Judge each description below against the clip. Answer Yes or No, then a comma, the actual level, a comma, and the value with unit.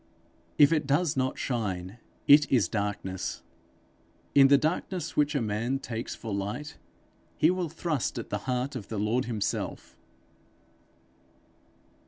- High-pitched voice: No, low, 125 Hz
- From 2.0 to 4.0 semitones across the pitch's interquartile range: No, wide, 5.6 semitones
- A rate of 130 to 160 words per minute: Yes, slow, 135 wpm